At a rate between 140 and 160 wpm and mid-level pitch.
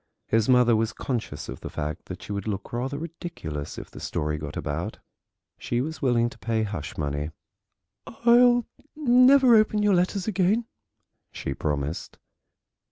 No: average, 155 wpm; low, 120 Hz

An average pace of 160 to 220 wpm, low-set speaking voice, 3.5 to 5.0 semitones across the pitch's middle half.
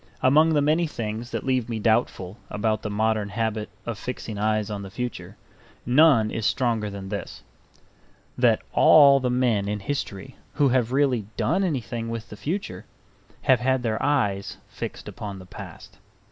Yes: average, 165 wpm; low, 115 Hz; average, 3.9 semitones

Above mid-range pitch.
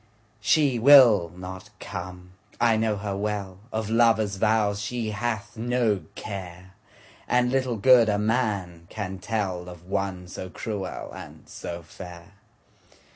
No: low, 105 Hz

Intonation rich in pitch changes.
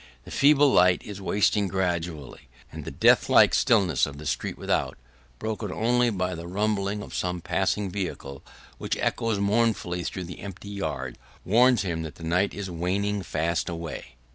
No: average, 3.6 semitones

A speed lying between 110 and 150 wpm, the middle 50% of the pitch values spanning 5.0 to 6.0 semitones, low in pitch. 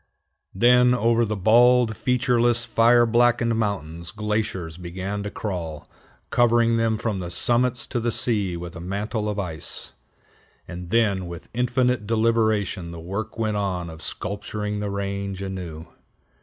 No: average, 140 wpm; average, 3.9 semitones; low, 105 Hz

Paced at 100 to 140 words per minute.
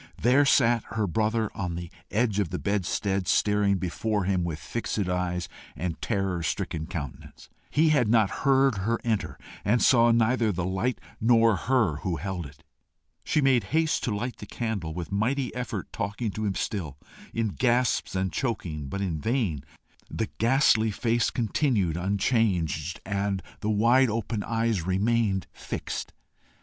No: average, 155 wpm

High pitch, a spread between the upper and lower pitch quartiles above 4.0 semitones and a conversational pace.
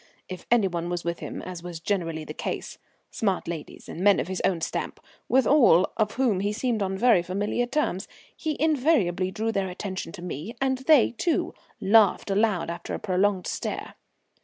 Yes: high, 195 Hz; average, 4.6 semitones; average, 185 wpm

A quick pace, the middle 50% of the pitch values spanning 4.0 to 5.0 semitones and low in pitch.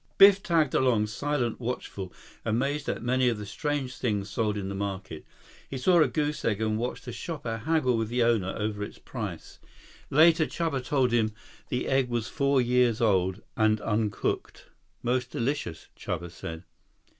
No: average, 165 wpm; average, 4.3 semitones; low, 120 Hz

